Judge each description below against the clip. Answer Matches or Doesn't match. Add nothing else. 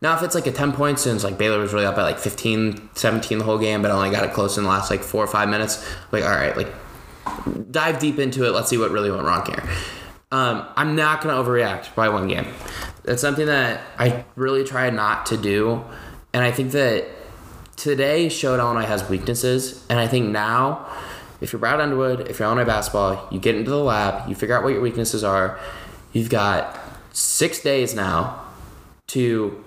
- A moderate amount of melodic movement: Matches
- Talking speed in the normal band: Doesn't match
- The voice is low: Matches